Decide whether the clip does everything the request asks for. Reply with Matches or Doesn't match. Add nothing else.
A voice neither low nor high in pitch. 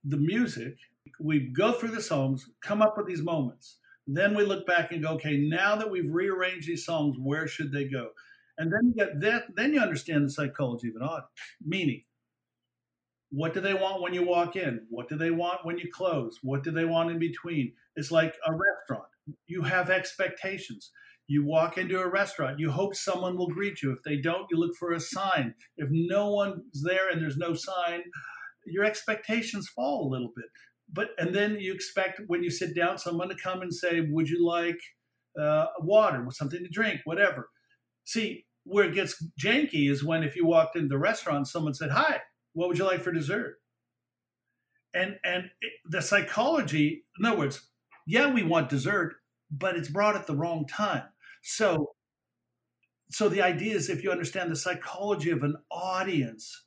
Matches